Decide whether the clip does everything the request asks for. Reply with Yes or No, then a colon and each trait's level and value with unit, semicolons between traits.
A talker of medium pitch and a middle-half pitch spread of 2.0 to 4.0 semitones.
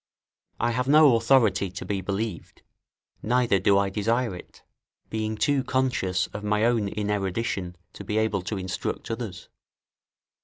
No: low, 105 Hz; average, 3.3 semitones